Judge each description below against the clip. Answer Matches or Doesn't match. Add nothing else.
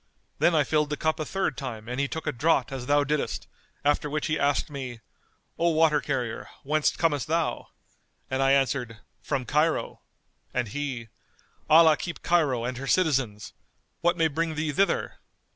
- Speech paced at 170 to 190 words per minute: Matches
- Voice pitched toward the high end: Doesn't match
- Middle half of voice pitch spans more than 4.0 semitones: Doesn't match